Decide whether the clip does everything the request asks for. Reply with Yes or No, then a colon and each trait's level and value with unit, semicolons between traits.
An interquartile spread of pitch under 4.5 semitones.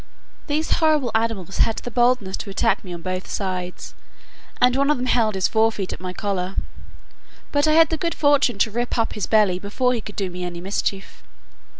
No: average, 4.9 semitones